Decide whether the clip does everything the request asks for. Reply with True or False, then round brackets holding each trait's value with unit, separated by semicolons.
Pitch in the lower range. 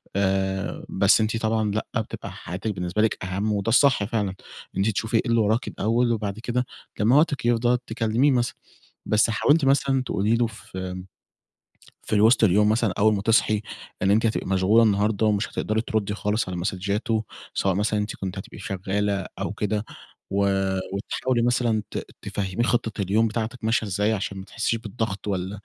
True (110 Hz)